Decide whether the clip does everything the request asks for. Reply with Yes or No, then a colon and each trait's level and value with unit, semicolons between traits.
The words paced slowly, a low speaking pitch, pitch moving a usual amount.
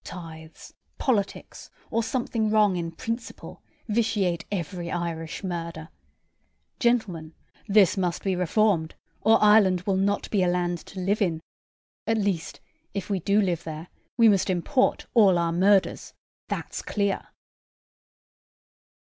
No: slow, 130 wpm; high, 190 Hz; average, 3.7 semitones